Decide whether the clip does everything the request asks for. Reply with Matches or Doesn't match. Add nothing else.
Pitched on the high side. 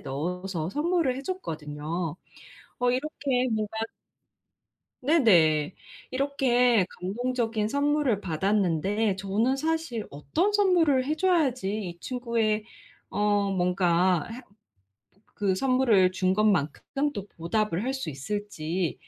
Matches